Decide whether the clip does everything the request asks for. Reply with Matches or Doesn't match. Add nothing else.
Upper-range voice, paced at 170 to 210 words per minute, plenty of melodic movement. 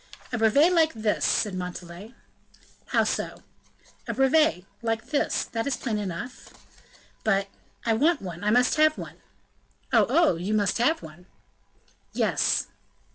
Doesn't match